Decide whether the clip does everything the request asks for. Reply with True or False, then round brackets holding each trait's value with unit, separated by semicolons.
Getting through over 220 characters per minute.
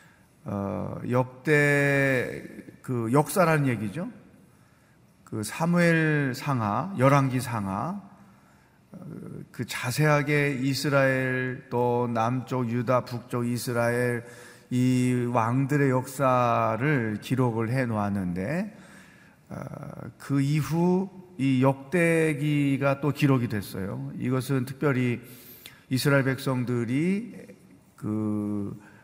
False (180 characters per minute)